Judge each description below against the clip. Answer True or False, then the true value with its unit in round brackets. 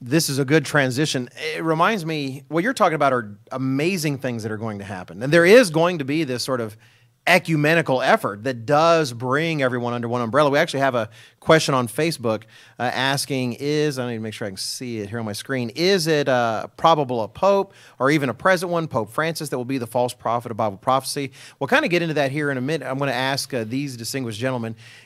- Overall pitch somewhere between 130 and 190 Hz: True (135 Hz)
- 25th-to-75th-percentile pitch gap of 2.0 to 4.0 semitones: False (4.4 semitones)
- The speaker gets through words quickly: True (240 wpm)